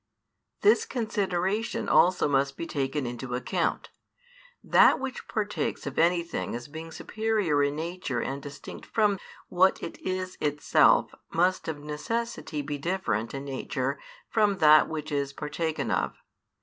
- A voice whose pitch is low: No, medium, 160 Hz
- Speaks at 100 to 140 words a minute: Yes, slow, 135 wpm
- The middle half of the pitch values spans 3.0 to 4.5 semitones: No, average, 4.9 semitones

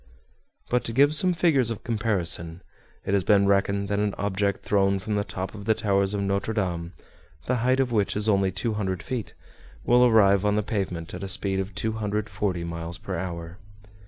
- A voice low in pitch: Yes, low, 100 Hz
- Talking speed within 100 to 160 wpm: No, average, 190 wpm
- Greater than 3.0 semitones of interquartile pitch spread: No, narrow, 2.6 semitones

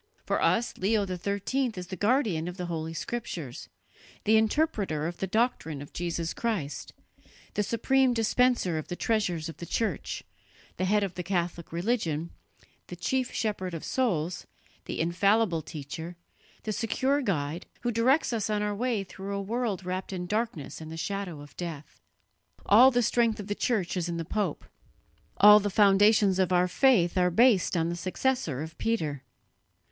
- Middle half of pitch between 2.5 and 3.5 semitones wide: No, average, 4.8 semitones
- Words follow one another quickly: No, average, 170 wpm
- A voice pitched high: Yes, high, 195 Hz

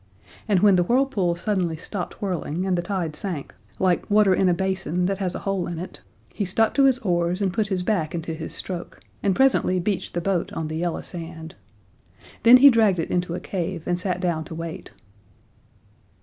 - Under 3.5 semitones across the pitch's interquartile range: Yes, narrow, 2.6 semitones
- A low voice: No, medium, 180 Hz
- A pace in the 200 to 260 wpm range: Yes, fast, 205 wpm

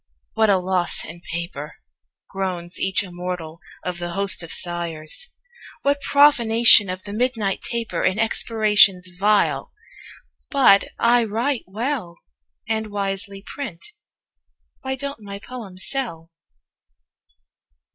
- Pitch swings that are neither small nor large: Yes, average, 4.5 semitones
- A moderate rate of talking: No, slow, 115 wpm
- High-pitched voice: Yes, high, 200 Hz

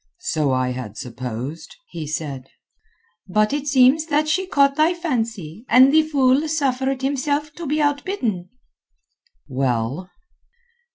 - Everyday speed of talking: No, slow, 125 wpm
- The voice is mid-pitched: No, very high, 260 Hz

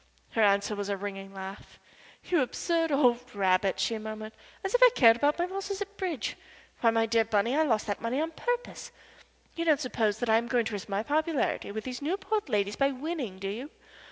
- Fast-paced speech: Yes, fast, 215 wpm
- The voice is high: Yes, high, 235 Hz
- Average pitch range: No, wide, 7.1 semitones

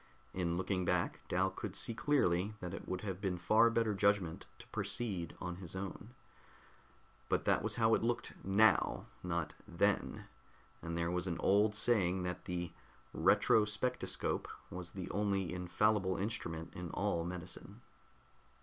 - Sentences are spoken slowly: No, average, 150 wpm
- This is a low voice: Yes, very low, 95 Hz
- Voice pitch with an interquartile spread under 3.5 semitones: Yes, average, 3.0 semitones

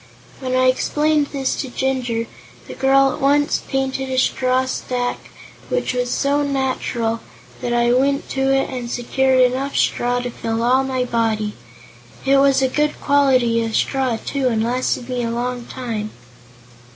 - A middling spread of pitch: No, narrow, 1.9 semitones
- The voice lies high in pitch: Yes, very high, 255 Hz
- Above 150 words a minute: Yes, average, 165 wpm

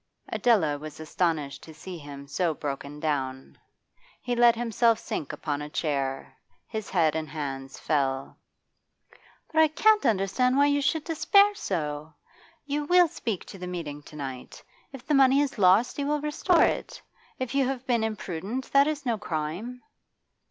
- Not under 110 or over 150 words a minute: No, average, 170 wpm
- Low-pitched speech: No, high, 190 Hz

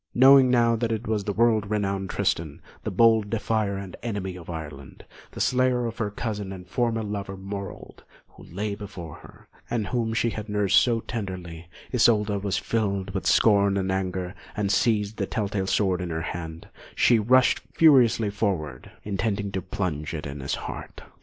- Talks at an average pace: Yes, average, 180 wpm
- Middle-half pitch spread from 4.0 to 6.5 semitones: No, average, 3.2 semitones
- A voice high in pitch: No, low, 100 Hz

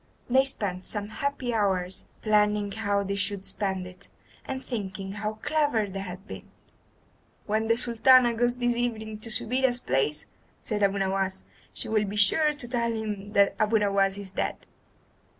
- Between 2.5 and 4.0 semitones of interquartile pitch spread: Yes, average, 3.3 semitones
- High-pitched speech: Yes, high, 210 Hz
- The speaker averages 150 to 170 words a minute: Yes, average, 165 wpm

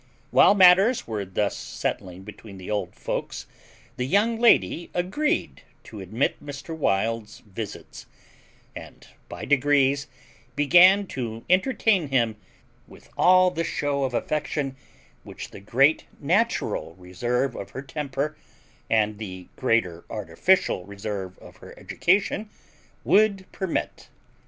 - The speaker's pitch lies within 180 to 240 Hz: No, low, 135 Hz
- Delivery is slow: Yes, slow, 120 wpm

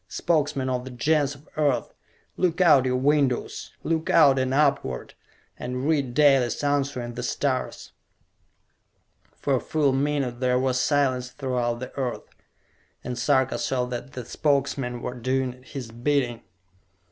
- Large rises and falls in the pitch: No, narrow, 2.4 semitones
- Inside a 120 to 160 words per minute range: Yes, average, 145 wpm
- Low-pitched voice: Yes, low, 130 Hz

